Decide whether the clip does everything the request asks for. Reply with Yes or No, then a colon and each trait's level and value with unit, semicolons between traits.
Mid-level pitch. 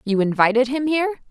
No: very high, 255 Hz